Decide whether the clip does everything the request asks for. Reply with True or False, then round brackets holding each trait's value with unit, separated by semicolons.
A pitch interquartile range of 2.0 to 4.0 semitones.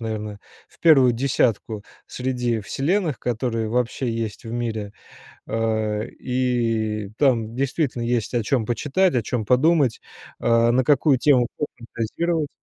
True (3.0 semitones)